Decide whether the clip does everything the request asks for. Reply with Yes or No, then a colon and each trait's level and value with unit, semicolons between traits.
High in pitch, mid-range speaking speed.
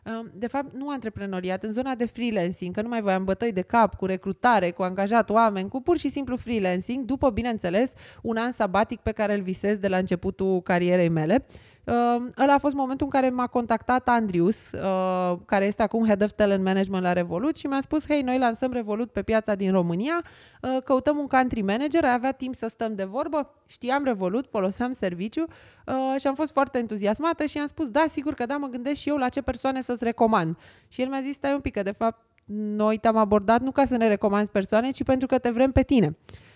No: high, 235 Hz; fast, 220 wpm